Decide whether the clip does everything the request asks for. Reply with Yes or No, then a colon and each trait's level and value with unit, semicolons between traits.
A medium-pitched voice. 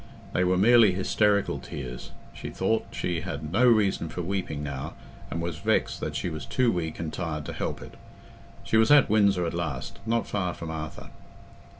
No: very low, 90 Hz